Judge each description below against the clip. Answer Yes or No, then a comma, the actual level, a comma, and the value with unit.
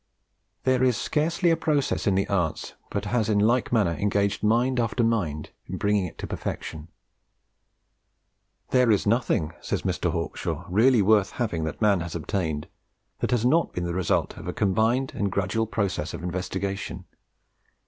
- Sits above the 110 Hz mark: No, low, 105 Hz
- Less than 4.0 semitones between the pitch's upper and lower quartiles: No, average, 4.7 semitones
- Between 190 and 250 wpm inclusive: No, average, 165 wpm